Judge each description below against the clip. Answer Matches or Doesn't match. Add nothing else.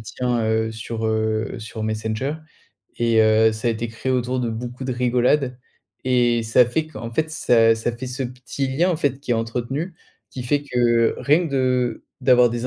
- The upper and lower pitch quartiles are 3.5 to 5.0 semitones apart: Doesn't match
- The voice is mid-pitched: Doesn't match